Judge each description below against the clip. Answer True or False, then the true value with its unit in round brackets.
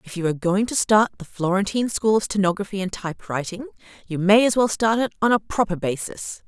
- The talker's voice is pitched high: True (200 Hz)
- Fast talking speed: True (215 wpm)